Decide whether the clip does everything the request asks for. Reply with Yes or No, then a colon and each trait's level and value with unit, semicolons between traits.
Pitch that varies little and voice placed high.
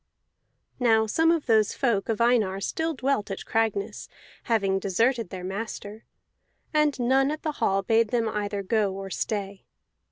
No: average, 3.7 semitones; high, 220 Hz